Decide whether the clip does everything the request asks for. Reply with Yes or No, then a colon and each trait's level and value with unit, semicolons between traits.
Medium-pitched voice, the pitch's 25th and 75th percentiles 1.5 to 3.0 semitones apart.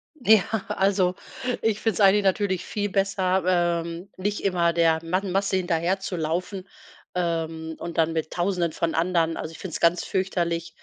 Yes: medium, 180 Hz; narrow, 2.6 semitones